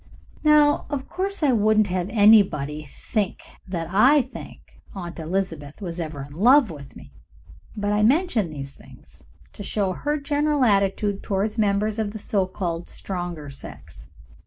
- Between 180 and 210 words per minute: No, average, 155 wpm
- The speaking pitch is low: No, high, 200 Hz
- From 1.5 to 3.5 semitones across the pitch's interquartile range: No, average, 5.1 semitones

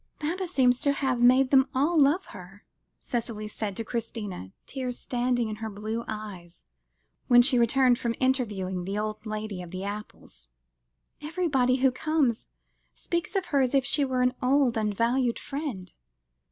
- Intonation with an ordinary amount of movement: Yes, average, 4.1 semitones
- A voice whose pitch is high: Yes, high, 245 Hz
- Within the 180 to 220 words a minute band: No, average, 165 wpm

